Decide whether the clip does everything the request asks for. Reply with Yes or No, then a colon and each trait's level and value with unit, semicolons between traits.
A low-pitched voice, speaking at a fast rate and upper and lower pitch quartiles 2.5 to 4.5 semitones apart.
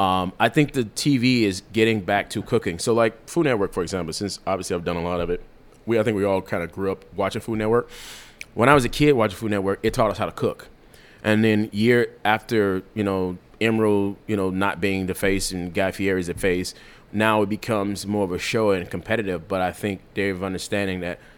Yes: low, 100 Hz; fast, 240 wpm; average, 2.8 semitones